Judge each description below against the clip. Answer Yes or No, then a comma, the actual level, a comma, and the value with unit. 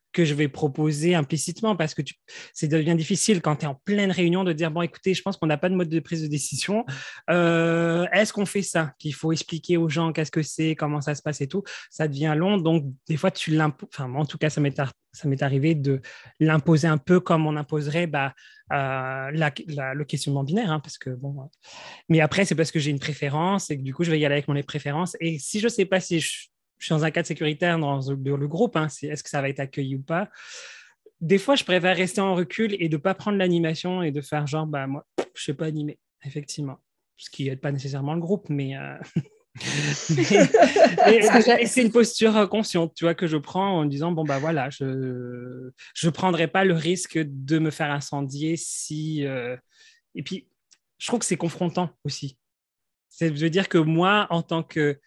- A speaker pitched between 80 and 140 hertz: No, medium, 160 Hz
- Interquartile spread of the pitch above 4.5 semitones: No, average, 3.6 semitones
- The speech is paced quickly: Yes, fast, 235 wpm